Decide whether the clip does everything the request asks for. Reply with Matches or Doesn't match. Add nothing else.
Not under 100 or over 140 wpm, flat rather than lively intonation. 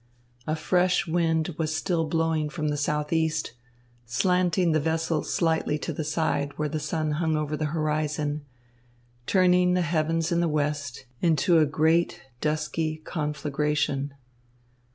Matches